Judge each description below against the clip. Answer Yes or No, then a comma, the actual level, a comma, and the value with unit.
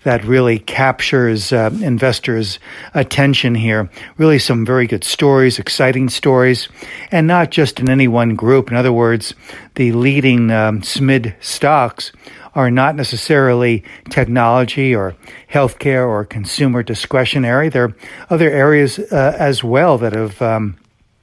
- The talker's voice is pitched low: Yes, low, 125 Hz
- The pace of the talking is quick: No, slow, 135 wpm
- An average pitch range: Yes, average, 3.0 semitones